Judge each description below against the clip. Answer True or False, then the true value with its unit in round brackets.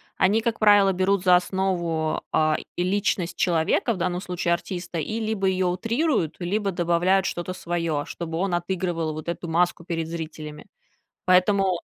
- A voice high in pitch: False (180 Hz)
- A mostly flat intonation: True (2.3 semitones)